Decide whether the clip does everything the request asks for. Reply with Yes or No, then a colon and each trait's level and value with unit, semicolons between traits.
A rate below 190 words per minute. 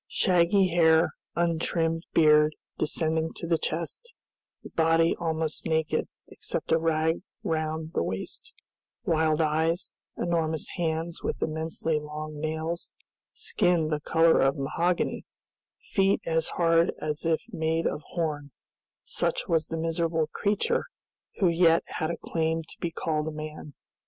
Yes: slow, 135 wpm